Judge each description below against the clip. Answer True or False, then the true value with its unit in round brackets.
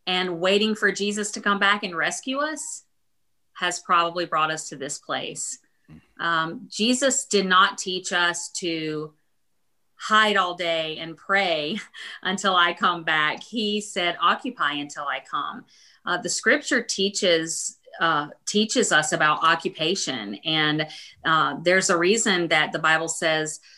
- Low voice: False (180 Hz)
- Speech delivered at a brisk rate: False (145 wpm)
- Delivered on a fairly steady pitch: False (4.3 semitones)